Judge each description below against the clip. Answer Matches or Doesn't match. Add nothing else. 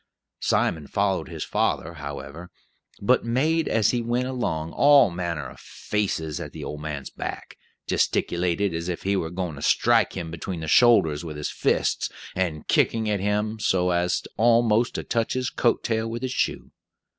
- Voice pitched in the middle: Doesn't match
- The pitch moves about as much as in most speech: Doesn't match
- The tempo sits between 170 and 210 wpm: Matches